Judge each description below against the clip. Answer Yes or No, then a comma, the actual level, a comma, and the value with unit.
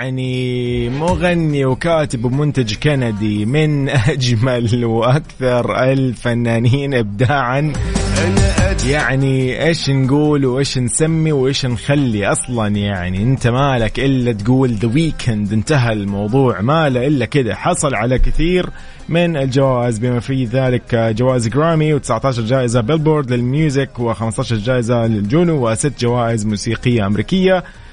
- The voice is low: Yes, low, 130 Hz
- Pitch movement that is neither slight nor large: Yes, average, 3.5 semitones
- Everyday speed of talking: No, slow, 110 wpm